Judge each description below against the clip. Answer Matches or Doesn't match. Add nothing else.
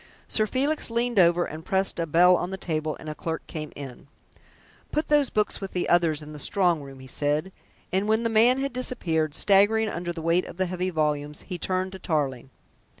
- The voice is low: Doesn't match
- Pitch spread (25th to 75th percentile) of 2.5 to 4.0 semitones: Doesn't match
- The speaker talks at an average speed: Doesn't match